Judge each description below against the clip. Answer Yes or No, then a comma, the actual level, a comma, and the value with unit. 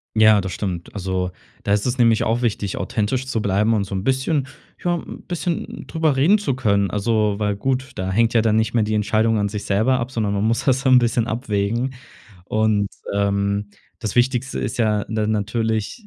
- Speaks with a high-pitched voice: No, low, 110 Hz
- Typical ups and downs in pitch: Yes, average, 3.5 semitones